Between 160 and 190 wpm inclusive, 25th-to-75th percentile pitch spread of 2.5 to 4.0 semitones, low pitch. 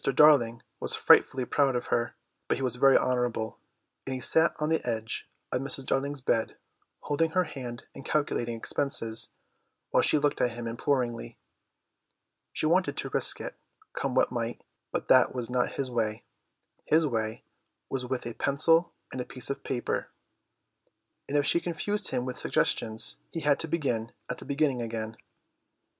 Yes: average, 170 wpm; average, 3.6 semitones; low, 130 Hz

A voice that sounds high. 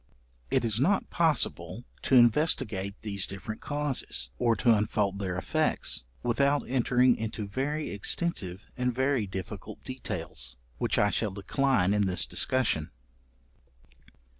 No: low, 110 Hz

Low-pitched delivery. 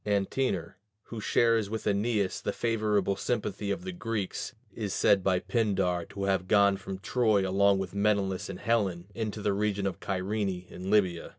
Yes: low, 100 Hz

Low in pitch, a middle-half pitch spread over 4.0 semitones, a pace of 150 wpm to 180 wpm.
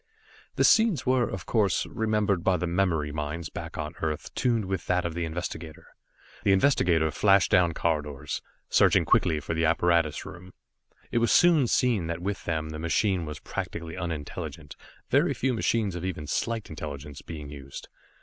Yes: very low, 85 Hz; average, 4.4 semitones; average, 170 wpm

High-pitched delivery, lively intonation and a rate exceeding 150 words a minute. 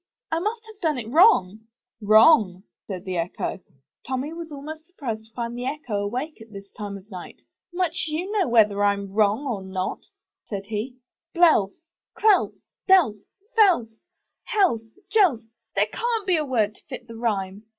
Yes: high, 240 Hz; wide, 8.2 semitones; average, 165 wpm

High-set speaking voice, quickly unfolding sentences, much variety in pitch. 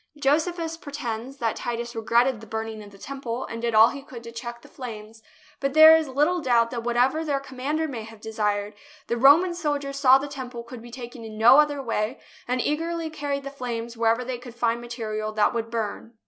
No: high, 245 Hz; fast, 210 wpm; average, 3.6 semitones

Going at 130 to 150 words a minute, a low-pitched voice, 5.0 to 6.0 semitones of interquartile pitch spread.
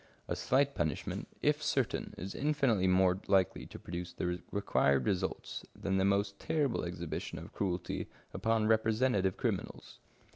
No: average, 140 wpm; very low, 95 Hz; average, 3.7 semitones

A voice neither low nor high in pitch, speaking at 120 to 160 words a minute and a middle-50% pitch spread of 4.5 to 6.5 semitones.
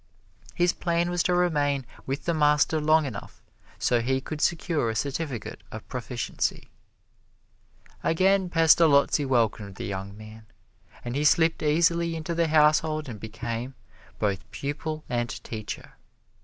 Yes: medium, 150 Hz; slow, 135 wpm; wide, 5.4 semitones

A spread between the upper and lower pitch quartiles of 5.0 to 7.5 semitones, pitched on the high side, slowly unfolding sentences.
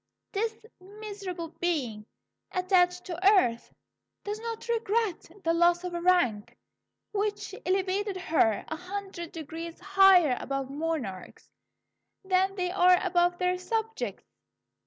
No: average, 3.1 semitones; very high, 365 Hz; slow, 115 wpm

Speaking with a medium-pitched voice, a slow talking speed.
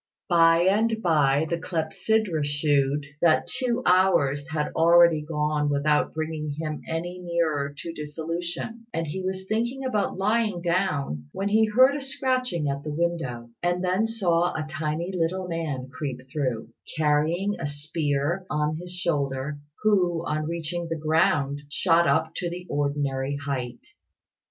No: medium, 165 Hz; average, 145 wpm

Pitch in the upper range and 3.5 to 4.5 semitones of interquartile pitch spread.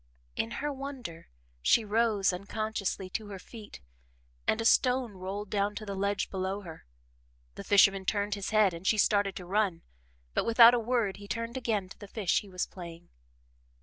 No: high, 205 Hz; average, 2.8 semitones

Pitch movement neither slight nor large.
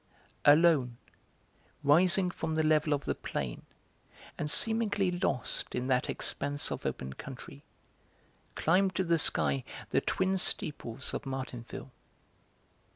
No: wide, 5.7 semitones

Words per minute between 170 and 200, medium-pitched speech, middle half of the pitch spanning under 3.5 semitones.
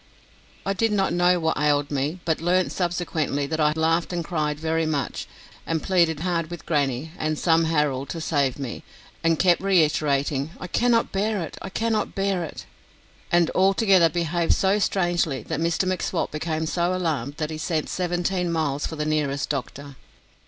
Yes: average, 175 wpm; medium, 165 Hz; average, 3.0 semitones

